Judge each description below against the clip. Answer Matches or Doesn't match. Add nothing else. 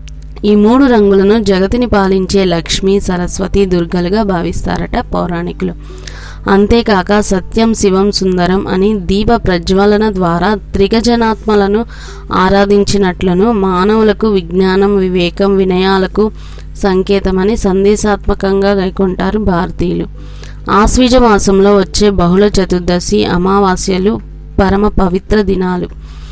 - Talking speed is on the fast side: Doesn't match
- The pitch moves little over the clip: Matches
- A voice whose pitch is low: Doesn't match